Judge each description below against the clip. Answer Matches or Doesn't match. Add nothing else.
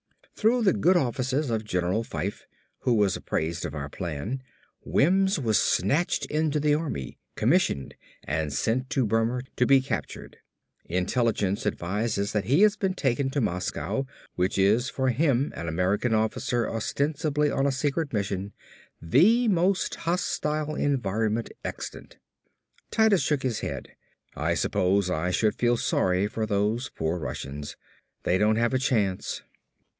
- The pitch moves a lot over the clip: Matches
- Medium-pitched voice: Doesn't match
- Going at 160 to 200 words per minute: Doesn't match